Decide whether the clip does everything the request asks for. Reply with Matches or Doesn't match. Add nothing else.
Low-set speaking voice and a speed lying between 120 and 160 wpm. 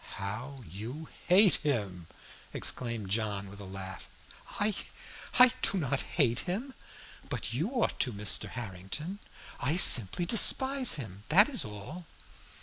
Matches